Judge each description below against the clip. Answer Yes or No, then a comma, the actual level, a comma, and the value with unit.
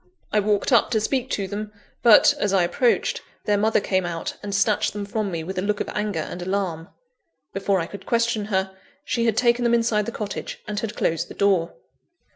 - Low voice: No, high, 205 Hz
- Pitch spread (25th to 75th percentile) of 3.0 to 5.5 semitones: No, narrow, 2.5 semitones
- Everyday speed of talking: No, fast, 215 wpm